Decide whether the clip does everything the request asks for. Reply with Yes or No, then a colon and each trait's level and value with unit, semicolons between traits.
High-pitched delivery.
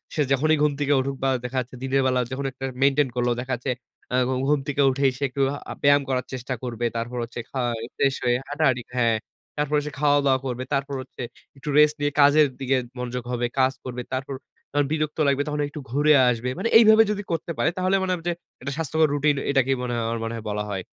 No: low, 135 Hz